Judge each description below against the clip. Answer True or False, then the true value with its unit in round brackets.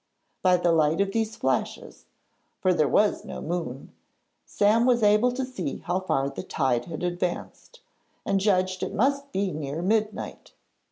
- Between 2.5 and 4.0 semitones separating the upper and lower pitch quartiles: False (4.7 semitones)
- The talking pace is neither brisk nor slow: True (160 wpm)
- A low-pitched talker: False (185 Hz)